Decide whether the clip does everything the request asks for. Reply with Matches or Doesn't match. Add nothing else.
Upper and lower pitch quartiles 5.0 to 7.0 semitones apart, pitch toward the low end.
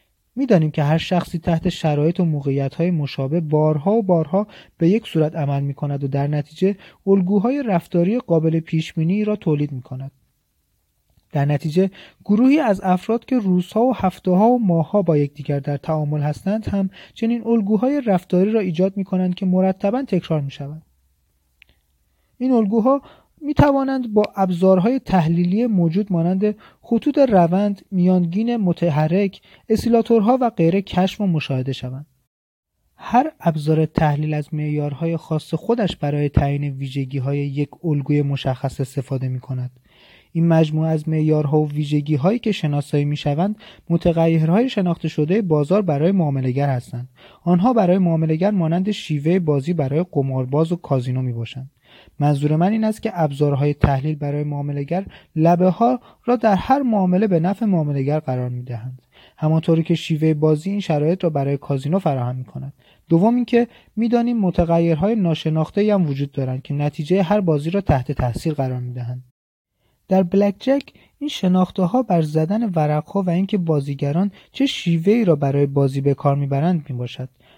Doesn't match